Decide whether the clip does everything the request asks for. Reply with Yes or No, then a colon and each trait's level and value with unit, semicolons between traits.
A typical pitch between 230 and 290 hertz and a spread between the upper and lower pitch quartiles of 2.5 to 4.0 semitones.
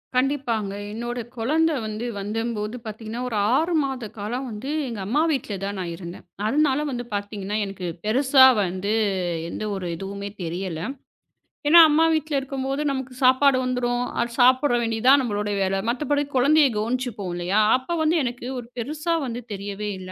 No: high, 240 Hz; average, 4.7 semitones